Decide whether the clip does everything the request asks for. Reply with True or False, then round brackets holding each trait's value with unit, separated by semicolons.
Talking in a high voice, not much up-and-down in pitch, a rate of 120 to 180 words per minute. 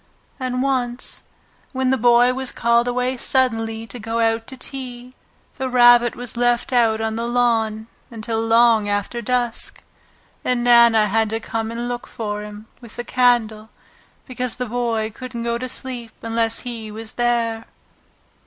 True (235 Hz; 1.6 semitones; 160 wpm)